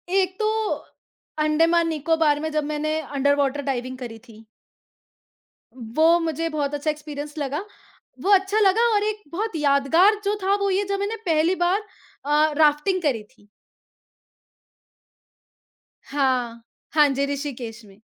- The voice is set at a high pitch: Yes, very high, 300 Hz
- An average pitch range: Yes, average, 3.9 semitones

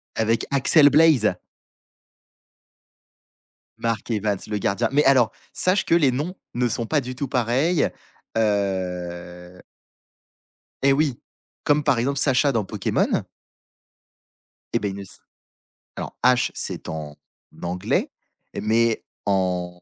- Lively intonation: Yes, wide, 6.0 semitones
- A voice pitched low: Yes, low, 115 Hz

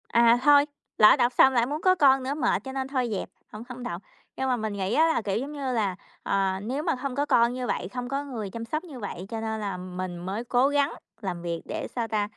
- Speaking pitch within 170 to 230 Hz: No, high, 240 Hz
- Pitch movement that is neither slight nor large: Yes, average, 5.0 semitones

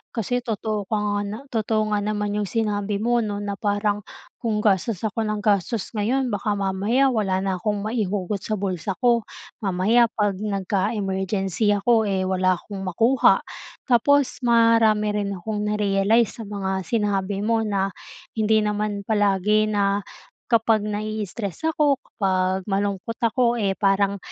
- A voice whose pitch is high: Yes, high, 210 Hz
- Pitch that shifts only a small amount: Yes, narrow, 2.1 semitones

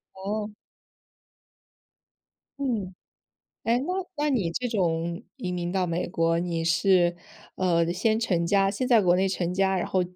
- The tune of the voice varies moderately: Yes, average, 3.9 semitones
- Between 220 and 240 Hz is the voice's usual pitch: No, medium, 185 Hz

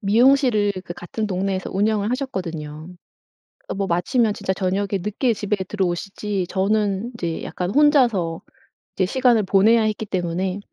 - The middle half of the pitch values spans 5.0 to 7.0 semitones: No, average, 3.2 semitones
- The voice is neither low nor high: No, high, 200 Hz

